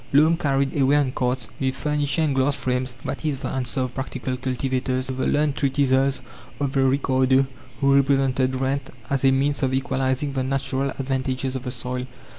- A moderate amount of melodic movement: No, narrow, 1.1 semitones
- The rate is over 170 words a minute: Yes, average, 185 wpm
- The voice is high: No, low, 135 Hz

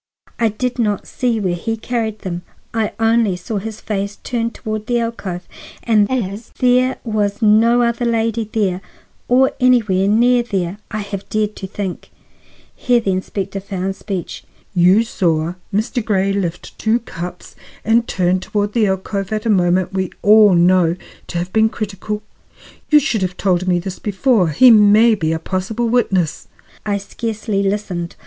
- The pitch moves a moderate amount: Yes, average, 3.4 semitones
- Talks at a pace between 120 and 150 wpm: No, average, 165 wpm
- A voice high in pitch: Yes, high, 210 Hz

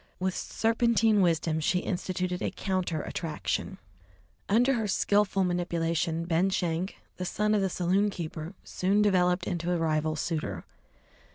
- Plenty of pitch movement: No, average, 3.1 semitones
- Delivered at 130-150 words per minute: Yes, slow, 135 wpm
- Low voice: No, medium, 180 Hz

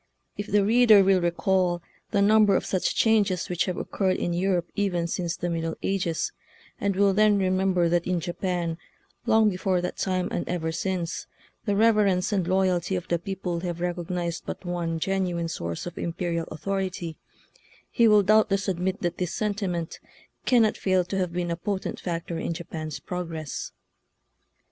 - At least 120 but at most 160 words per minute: No, average, 170 wpm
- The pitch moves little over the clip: Yes, narrow, 2.3 semitones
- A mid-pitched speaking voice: Yes, medium, 180 Hz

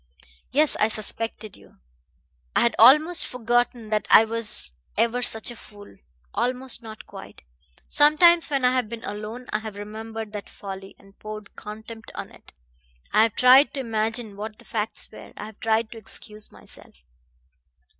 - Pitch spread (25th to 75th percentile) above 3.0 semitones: No, narrow, 2.6 semitones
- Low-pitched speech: No, high, 225 Hz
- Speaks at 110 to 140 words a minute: No, average, 165 wpm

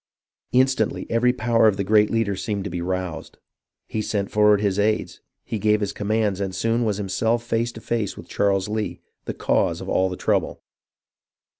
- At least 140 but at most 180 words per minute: No, average, 190 wpm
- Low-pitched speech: Yes, low, 105 Hz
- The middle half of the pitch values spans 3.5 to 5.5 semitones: No, narrow, 2.4 semitones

